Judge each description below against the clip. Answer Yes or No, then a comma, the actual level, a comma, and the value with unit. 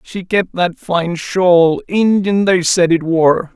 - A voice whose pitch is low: No, medium, 180 Hz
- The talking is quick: No, average, 170 wpm